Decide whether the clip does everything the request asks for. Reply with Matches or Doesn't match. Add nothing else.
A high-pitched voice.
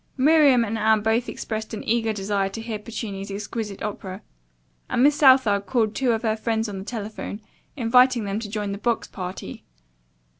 Matches